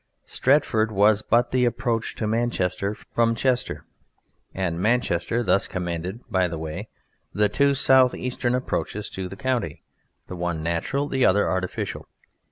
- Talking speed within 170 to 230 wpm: No, average, 145 wpm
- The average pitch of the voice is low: Yes, low, 105 Hz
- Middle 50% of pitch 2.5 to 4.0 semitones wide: No, average, 5.2 semitones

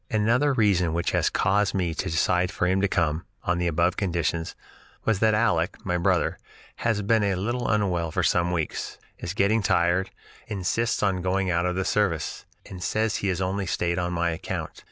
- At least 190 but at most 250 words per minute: Yes, average, 195 wpm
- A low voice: Yes, very low, 95 Hz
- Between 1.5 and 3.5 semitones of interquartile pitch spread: Yes, average, 3.1 semitones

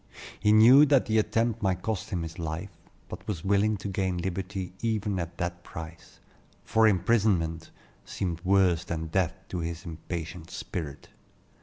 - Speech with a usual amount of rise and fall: Yes, average, 3.8 semitones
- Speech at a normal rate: Yes, average, 155 wpm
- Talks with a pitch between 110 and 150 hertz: No, very low, 95 Hz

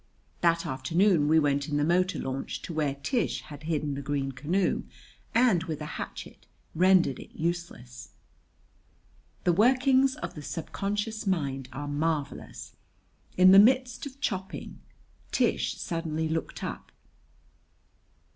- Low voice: No, medium, 165 Hz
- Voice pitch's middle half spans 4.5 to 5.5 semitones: Yes, average, 5.1 semitones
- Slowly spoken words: Yes, slow, 130 wpm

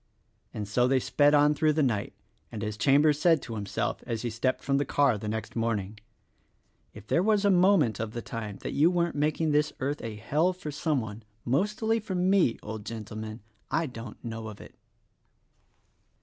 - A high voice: No, low, 130 Hz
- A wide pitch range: Yes, wide, 6.1 semitones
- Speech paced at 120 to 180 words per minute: No, average, 195 wpm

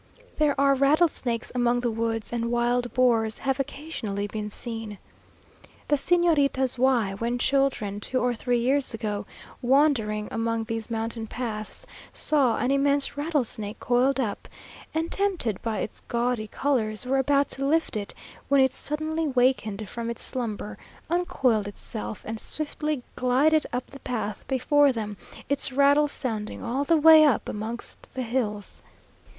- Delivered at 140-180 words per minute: Yes, average, 145 wpm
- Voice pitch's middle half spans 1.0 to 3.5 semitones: No, average, 3.9 semitones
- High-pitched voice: Yes, high, 245 Hz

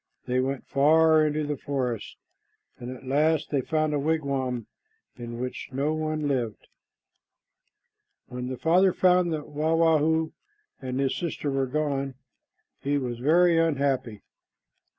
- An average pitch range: Yes, average, 3.4 semitones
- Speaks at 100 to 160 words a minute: Yes, average, 140 wpm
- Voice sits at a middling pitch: Yes, medium, 145 Hz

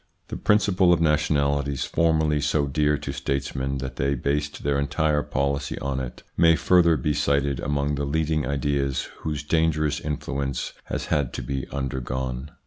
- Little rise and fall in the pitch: Yes, narrow, 1.9 semitones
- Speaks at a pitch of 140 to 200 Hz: No, very low, 70 Hz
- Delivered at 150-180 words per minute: Yes, average, 155 wpm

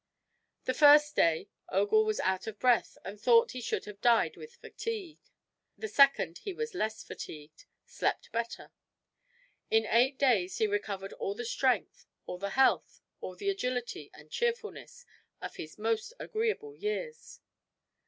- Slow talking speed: No, average, 150 wpm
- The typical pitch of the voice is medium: No, high, 245 Hz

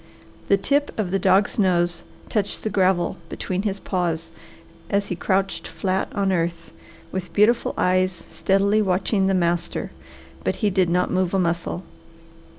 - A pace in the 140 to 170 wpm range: Yes, average, 155 wpm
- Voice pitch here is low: No, high, 190 Hz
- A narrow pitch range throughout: Yes, narrow, 1.9 semitones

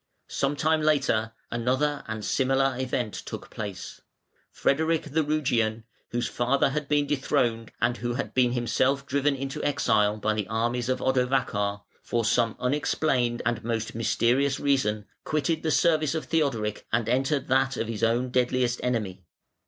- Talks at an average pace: Yes, average, 155 wpm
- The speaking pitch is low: Yes, low, 125 Hz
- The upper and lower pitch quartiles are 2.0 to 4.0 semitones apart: Yes, average, 3.5 semitones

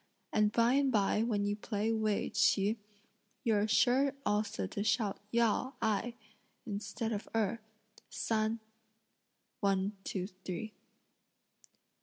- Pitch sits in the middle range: No, high, 215 Hz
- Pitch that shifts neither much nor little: No, narrow, 2.1 semitones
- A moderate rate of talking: No, slow, 120 wpm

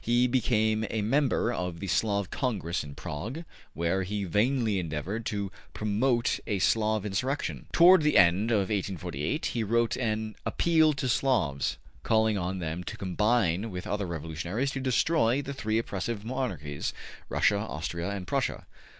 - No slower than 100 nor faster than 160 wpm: Yes, average, 150 wpm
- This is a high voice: No, low, 105 Hz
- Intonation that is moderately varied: Yes, average, 4.9 semitones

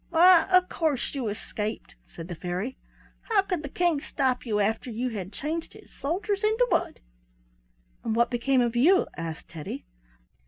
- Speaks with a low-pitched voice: No, very high, 260 Hz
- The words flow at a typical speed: Yes, average, 165 wpm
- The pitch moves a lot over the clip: Yes, wide, 8.0 semitones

